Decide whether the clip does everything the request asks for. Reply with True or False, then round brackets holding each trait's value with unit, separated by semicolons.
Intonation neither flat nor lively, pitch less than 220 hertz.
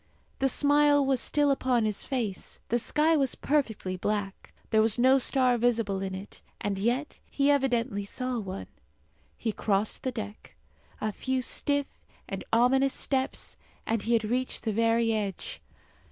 False (4.1 semitones; 240 Hz)